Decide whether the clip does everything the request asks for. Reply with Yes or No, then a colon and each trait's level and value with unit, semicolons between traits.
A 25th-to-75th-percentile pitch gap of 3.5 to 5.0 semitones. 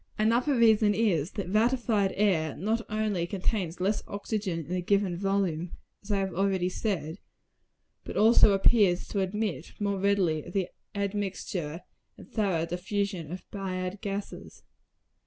No: average, 2.7 semitones